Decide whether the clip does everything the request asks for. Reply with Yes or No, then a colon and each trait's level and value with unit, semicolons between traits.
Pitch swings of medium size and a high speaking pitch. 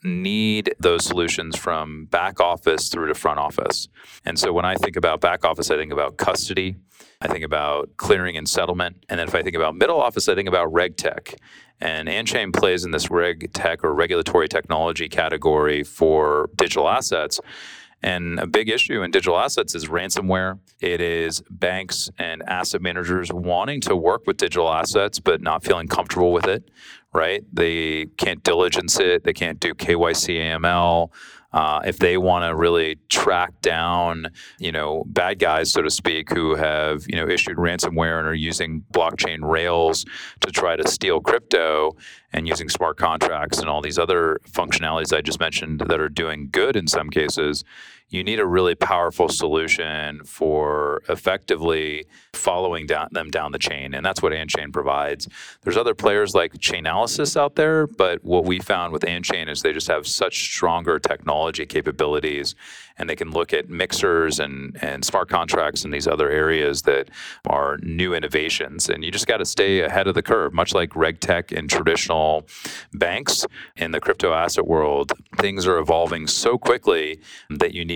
No: average, 3.5 semitones; very low, 85 Hz